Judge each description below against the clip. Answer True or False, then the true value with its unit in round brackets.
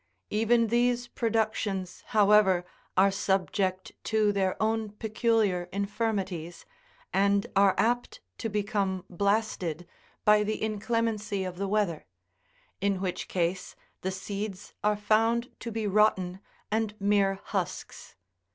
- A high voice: True (205 Hz)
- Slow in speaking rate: True (115 wpm)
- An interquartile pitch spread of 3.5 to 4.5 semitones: False (2.4 semitones)